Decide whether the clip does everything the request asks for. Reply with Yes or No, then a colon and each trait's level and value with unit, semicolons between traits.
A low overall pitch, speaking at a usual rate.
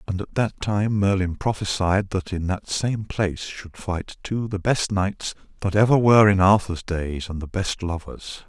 Yes: very low, 95 Hz; average, 190 wpm